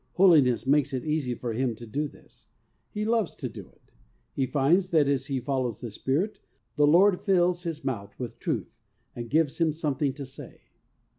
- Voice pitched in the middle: Yes, medium, 145 Hz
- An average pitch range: Yes, average, 4.6 semitones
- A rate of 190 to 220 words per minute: Yes, average, 195 wpm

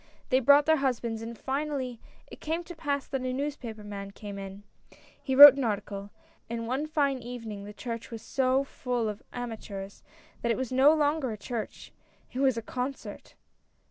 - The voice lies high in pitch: Yes, very high, 250 Hz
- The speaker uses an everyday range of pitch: Yes, average, 3.9 semitones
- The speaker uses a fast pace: No, average, 185 wpm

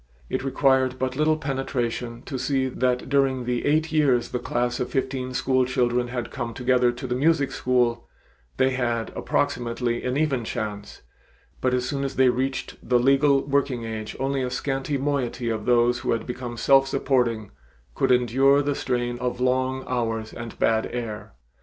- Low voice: Yes, low, 125 Hz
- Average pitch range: No, narrow, 1.9 semitones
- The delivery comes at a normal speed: Yes, average, 170 wpm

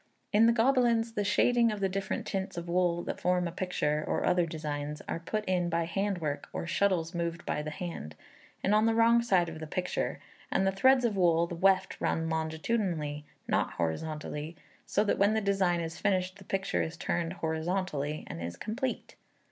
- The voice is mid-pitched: Yes, medium, 180 Hz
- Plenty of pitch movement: No, average, 3.9 semitones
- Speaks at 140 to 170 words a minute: No, average, 195 wpm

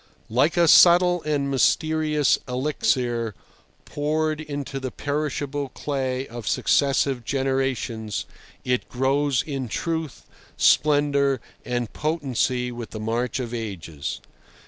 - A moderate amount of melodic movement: Yes, average, 3.3 semitones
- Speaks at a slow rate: Yes, slow, 105 wpm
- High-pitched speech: No, low, 135 Hz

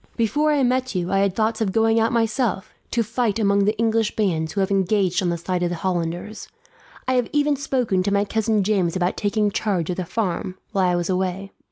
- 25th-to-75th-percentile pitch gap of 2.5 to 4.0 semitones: Yes, average, 3.5 semitones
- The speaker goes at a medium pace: No, fast, 225 wpm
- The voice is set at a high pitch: Yes, high, 200 Hz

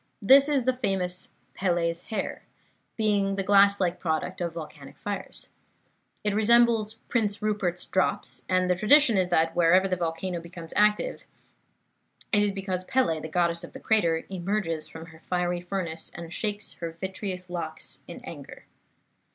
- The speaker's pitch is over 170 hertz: Yes, medium, 185 Hz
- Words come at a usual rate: Yes, average, 155 wpm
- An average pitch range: Yes, average, 3.5 semitones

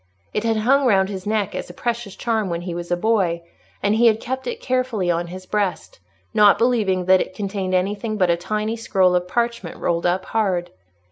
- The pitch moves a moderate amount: Yes, average, 3.7 semitones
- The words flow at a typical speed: No, fast, 210 wpm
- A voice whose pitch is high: Yes, high, 200 Hz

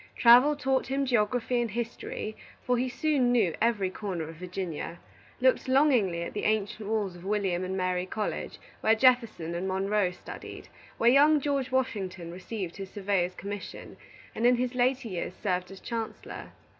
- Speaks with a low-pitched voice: No, high, 215 Hz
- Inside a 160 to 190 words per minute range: Yes, average, 165 wpm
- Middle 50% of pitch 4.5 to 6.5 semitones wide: Yes, average, 5.1 semitones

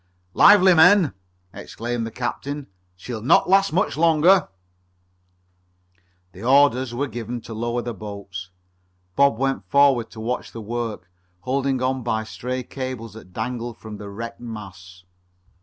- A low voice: Yes, low, 120 Hz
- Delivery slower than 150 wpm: Yes, average, 140 wpm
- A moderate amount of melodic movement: Yes, average, 3.8 semitones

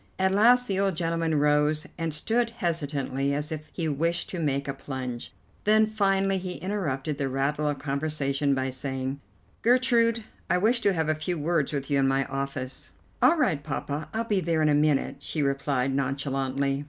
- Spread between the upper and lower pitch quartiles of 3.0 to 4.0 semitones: No, average, 5.2 semitones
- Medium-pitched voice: Yes, medium, 150 Hz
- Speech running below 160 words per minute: No, average, 185 wpm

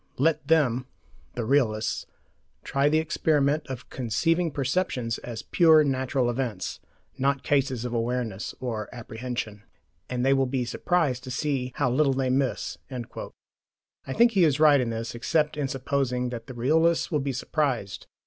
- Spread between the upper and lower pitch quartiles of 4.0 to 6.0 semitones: No, average, 3.4 semitones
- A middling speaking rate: Yes, average, 155 wpm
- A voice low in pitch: Yes, low, 130 Hz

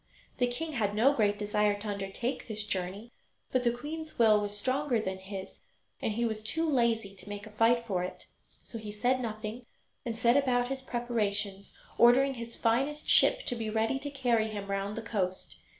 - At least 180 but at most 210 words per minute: Yes, average, 195 wpm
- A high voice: Yes, high, 225 Hz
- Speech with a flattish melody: No, average, 3.0 semitones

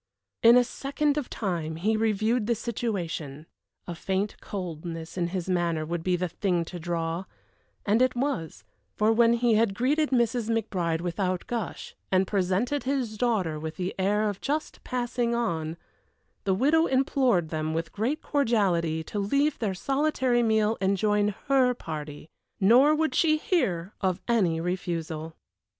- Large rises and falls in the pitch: Yes, wide, 5.9 semitones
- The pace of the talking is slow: No, average, 155 wpm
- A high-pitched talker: Yes, high, 205 Hz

